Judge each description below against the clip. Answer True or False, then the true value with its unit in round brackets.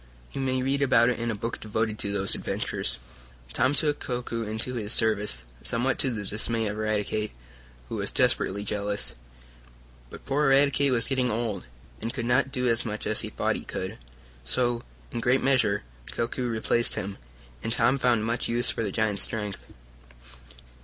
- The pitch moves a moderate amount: True (3.0 semitones)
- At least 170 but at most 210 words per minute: True (180 wpm)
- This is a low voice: True (115 Hz)